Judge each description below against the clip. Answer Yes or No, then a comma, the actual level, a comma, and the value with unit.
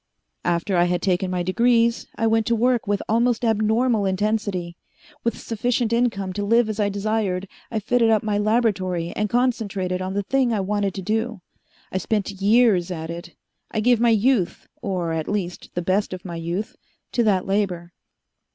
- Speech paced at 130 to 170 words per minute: No, average, 180 wpm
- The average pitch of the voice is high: Yes, high, 205 Hz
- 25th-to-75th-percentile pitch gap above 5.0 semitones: No, average, 3.6 semitones